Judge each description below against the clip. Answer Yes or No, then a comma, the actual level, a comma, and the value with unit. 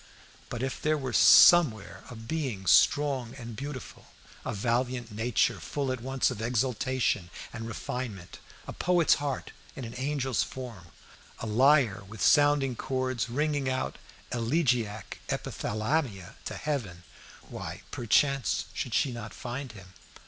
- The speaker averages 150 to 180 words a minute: No, slow, 135 wpm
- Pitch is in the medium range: No, low, 125 Hz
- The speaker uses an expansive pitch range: No, average, 3.5 semitones